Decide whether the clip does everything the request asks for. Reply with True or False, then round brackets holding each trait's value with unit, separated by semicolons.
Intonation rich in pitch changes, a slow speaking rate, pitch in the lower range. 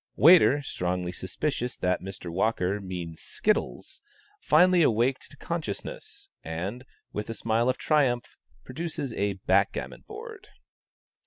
True (7.3 semitones; 115 wpm; 115 Hz)